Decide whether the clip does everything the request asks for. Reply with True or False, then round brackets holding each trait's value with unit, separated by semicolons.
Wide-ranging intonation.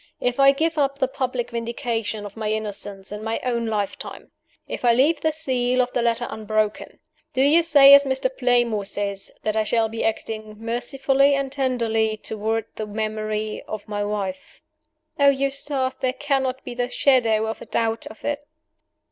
False (3.8 semitones)